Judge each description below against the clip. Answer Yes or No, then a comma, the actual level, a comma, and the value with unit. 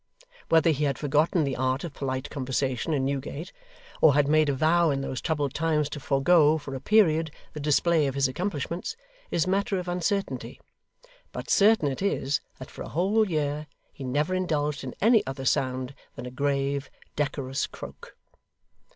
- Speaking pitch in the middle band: Yes, medium, 145 Hz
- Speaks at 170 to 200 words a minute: Yes, average, 175 wpm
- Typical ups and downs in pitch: Yes, average, 3.6 semitones